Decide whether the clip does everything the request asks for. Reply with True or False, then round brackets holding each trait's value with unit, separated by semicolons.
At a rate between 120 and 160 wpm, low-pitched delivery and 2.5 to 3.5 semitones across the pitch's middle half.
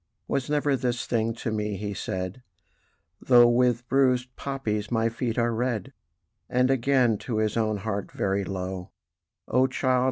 True (155 wpm; 120 Hz; 3.2 semitones)